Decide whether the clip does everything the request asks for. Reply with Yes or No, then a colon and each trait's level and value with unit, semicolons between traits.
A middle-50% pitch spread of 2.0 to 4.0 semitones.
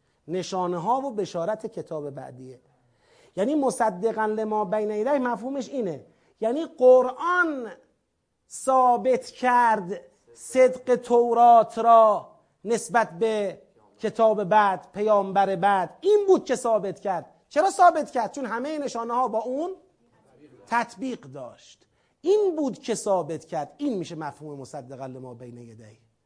No: average, 5.1 semitones